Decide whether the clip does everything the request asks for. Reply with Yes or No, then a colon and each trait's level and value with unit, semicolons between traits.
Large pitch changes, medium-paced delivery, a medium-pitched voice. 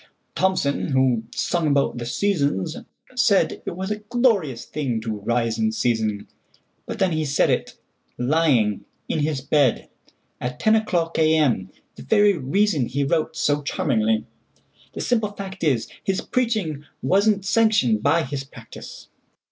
No: wide, 7.8 semitones; slow, 125 wpm; medium, 150 Hz